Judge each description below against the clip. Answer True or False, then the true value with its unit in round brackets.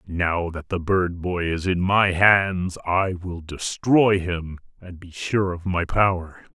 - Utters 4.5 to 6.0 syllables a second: False (3.6 syllables/s)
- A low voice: True (90 Hz)